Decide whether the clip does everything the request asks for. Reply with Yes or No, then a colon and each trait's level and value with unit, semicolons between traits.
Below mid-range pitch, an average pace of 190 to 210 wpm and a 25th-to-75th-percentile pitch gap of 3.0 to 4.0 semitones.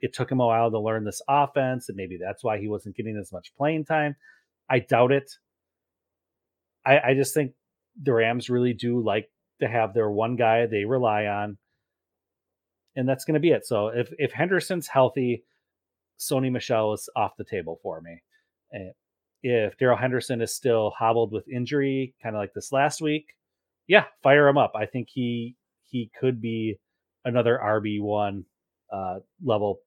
No: low, 120 Hz; average, 180 wpm; average, 3.7 semitones